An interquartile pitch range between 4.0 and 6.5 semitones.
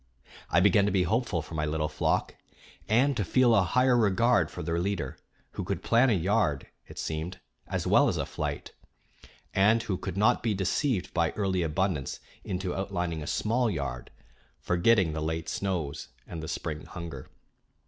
Yes: average, 4.8 semitones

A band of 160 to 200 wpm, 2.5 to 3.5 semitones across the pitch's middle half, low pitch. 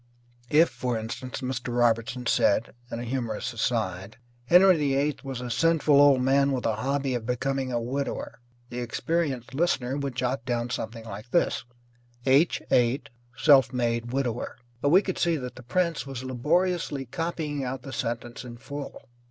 Yes: average, 165 wpm; average, 3.1 semitones; low, 130 Hz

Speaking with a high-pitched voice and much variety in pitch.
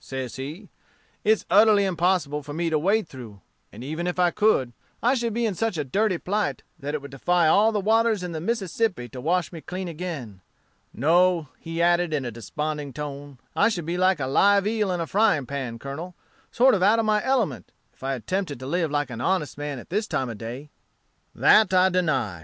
No: medium, 170 Hz; wide, 6.0 semitones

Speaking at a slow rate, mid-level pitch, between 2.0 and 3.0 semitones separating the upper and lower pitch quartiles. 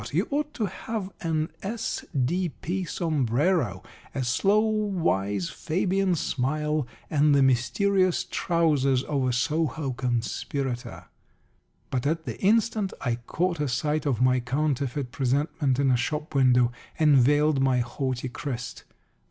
No: slow, 125 wpm; medium, 145 Hz; average, 5.2 semitones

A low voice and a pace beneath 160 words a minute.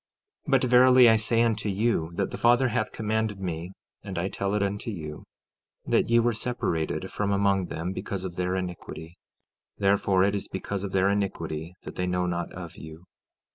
No: low, 100 Hz; average, 190 wpm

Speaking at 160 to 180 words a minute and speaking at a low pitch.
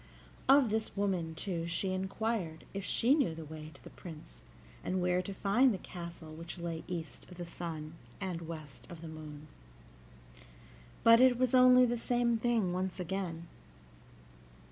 No: average, 165 wpm; medium, 180 Hz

